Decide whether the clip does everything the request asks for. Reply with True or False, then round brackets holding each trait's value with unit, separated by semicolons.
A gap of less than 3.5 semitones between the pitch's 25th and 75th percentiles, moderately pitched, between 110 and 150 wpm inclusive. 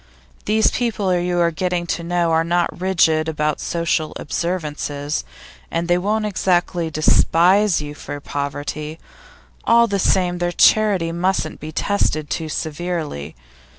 True (2.9 semitones; 170 Hz; 135 wpm)